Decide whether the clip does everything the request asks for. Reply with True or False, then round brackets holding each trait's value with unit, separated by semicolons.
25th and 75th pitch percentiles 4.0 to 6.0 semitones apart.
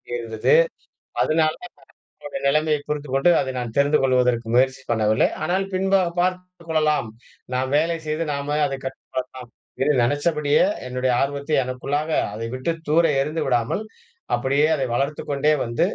False (3.4 semitones)